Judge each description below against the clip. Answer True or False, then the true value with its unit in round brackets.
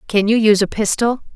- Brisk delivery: True (220 wpm)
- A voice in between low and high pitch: False (215 Hz)